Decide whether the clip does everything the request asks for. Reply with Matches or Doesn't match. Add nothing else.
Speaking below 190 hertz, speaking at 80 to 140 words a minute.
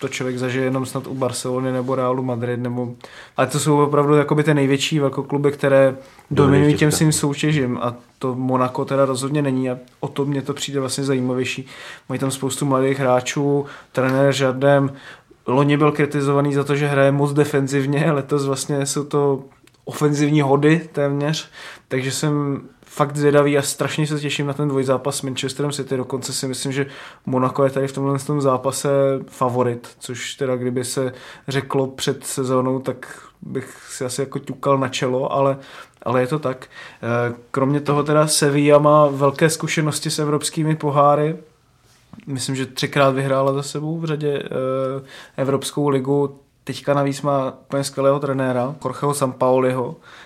Doesn't match